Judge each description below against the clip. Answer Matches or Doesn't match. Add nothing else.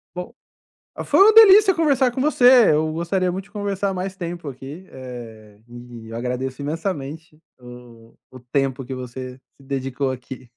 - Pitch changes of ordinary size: Doesn't match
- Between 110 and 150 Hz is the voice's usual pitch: Matches